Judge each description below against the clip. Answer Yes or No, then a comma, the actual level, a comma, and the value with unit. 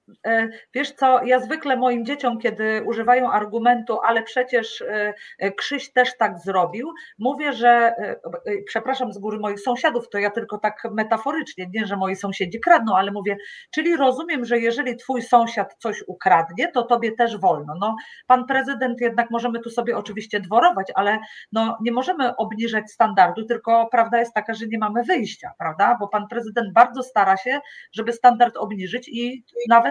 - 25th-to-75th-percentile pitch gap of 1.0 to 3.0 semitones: Yes, narrow, 2.6 semitones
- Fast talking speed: Yes, fast, 165 wpm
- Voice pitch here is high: Yes, high, 235 Hz